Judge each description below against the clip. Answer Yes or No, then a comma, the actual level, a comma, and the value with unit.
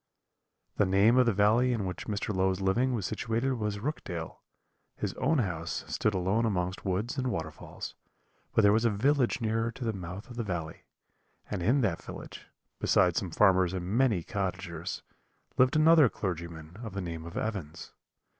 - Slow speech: No, average, 175 wpm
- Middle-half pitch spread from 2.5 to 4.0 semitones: No, average, 4.4 semitones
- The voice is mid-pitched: No, low, 100 Hz